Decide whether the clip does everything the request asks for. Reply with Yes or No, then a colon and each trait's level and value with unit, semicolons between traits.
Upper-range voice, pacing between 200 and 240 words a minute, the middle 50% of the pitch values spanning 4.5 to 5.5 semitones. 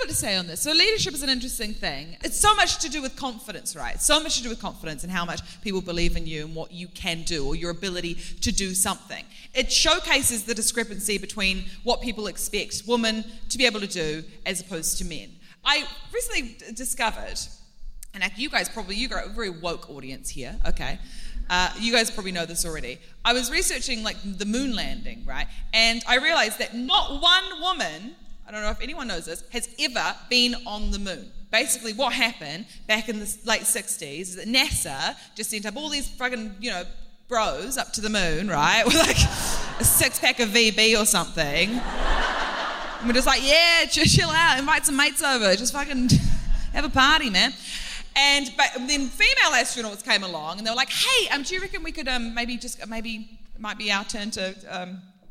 Yes: high, 225 Hz; fast, 205 wpm; average, 5.1 semitones